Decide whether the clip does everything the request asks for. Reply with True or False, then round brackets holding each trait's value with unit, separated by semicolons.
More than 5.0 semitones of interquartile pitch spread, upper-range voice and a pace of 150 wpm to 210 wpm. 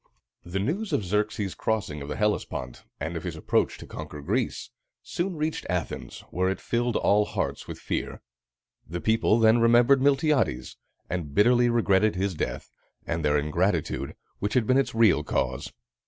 False (5.5 semitones; 105 Hz; 165 wpm)